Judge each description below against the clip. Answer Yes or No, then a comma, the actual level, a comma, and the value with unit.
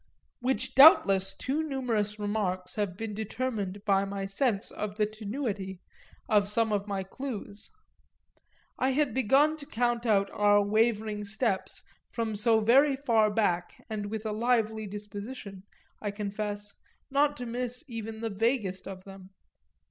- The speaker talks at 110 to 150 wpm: Yes, average, 140 wpm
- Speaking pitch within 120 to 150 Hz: No, high, 215 Hz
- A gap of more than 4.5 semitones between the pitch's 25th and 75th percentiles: No, average, 3.1 semitones